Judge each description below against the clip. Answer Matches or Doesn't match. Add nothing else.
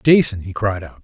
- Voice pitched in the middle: Doesn't match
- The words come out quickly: Matches